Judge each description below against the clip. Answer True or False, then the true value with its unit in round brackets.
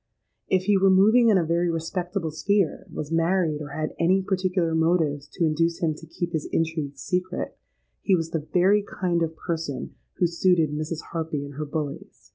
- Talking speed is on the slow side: False (185 wpm)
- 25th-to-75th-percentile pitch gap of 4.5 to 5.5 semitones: False (2.9 semitones)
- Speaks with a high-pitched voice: False (165 Hz)